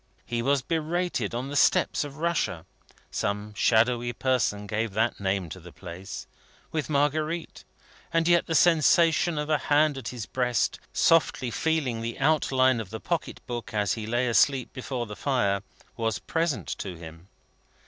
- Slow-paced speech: No, average, 160 wpm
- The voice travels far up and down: Yes, wide, 6.2 semitones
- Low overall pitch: Yes, low, 125 Hz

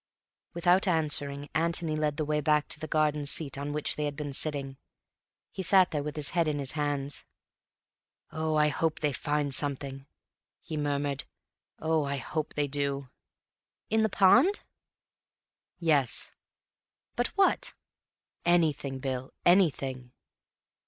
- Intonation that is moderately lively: No, narrow, 2.2 semitones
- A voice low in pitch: No, medium, 150 Hz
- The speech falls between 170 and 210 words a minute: No, average, 140 wpm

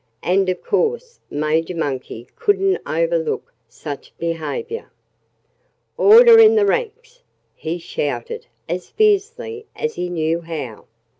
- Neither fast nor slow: No, slow, 115 wpm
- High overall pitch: Yes, very high, 385 Hz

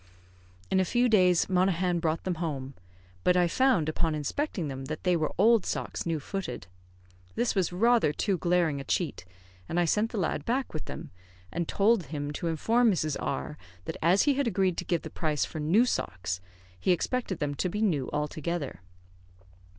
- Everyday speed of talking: Yes, average, 190 wpm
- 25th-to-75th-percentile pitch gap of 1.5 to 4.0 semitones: No, average, 4.5 semitones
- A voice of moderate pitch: Yes, medium, 175 Hz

